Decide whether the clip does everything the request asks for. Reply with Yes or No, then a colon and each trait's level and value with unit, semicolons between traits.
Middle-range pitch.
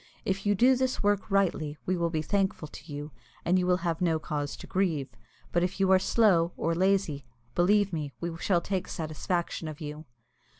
Yes: medium, 175 Hz